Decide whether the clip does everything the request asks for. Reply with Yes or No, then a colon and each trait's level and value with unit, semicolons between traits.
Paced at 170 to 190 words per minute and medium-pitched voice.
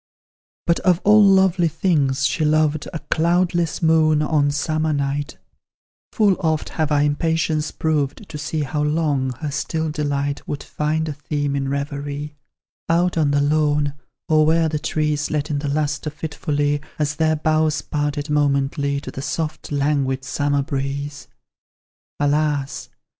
No: average, 145 wpm; medium, 150 Hz